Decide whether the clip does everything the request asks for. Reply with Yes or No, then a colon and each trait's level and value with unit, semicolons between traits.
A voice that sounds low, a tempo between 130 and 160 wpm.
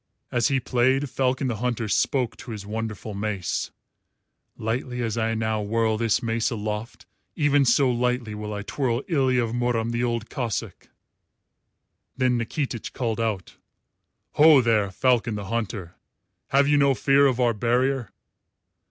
Yes: low, 120 Hz; average, 150 wpm